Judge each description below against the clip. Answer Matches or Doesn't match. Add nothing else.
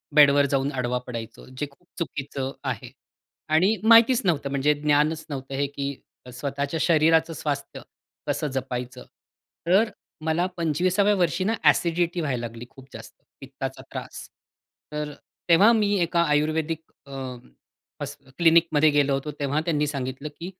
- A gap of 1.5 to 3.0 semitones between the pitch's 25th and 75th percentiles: Doesn't match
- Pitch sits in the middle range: Matches